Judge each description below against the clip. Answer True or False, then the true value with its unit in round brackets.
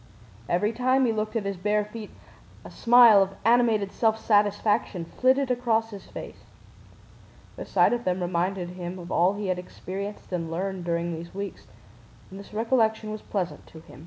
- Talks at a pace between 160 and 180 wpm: True (175 wpm)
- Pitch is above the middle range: True (205 Hz)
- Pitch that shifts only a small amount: False (3.7 semitones)